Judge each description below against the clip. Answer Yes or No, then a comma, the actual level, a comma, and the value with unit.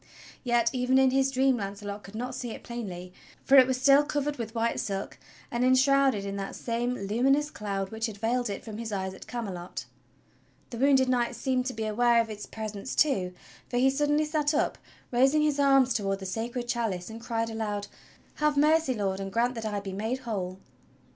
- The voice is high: Yes, high, 235 Hz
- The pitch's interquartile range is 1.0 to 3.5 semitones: No, average, 4.3 semitones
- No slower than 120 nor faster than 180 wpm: No, average, 200 wpm